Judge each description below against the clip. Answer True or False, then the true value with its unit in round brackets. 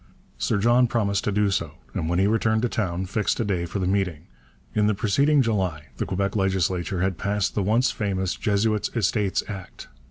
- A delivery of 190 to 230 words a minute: True (195 wpm)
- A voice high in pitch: False (100 Hz)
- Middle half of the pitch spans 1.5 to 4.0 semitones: True (2.6 semitones)